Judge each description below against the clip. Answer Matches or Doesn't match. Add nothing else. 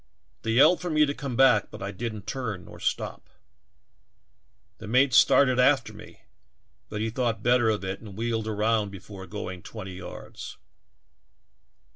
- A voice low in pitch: Matches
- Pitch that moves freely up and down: Doesn't match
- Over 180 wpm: Doesn't match